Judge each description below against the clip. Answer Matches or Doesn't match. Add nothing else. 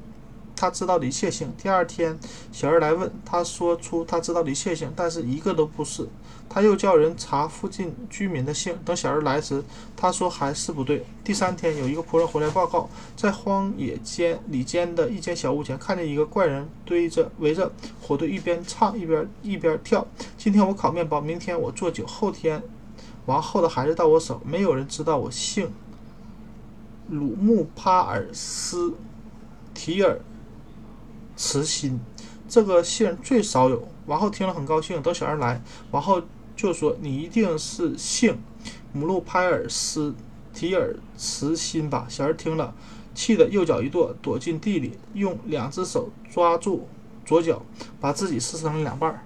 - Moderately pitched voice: Matches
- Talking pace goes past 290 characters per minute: Doesn't match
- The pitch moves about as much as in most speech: Matches